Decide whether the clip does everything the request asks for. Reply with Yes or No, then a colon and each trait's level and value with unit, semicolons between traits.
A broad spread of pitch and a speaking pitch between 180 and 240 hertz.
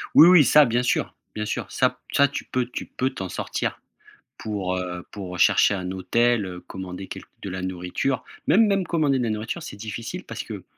No: wide, 6.4 semitones; low, 110 Hz